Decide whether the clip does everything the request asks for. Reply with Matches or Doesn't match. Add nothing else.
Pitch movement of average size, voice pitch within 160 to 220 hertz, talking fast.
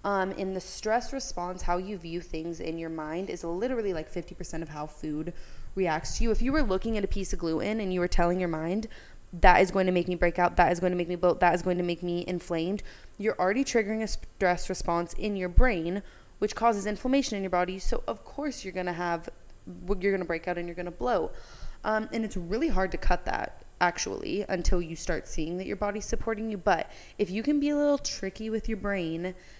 Matches